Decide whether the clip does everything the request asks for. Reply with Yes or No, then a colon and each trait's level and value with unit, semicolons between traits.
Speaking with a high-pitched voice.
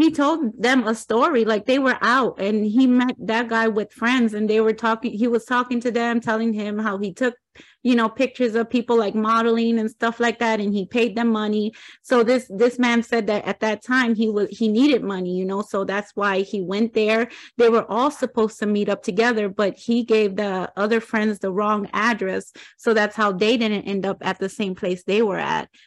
Yes: high, 225 Hz